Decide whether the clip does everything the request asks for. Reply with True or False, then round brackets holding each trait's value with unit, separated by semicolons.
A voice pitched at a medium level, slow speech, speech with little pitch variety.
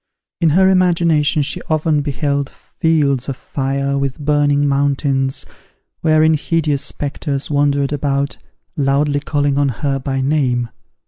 True (145 Hz; 125 wpm; 1.6 semitones)